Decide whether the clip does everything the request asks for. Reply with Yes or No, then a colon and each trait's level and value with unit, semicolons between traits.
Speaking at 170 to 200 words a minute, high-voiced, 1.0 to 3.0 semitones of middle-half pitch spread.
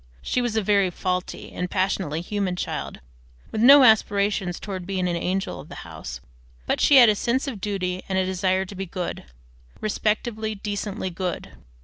Yes: average, 175 wpm; high, 195 Hz; narrow, 2.6 semitones